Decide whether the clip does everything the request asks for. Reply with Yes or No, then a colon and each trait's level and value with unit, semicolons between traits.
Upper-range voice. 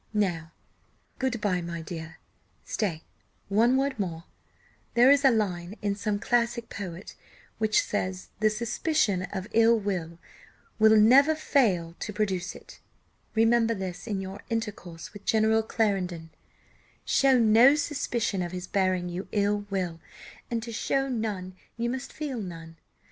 Yes: high, 210 Hz